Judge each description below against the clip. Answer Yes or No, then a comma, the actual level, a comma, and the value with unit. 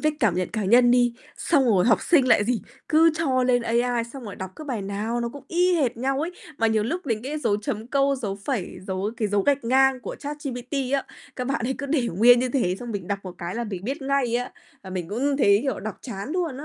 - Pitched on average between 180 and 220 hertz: No, high, 245 Hz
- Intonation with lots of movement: No, average, 4.7 semitones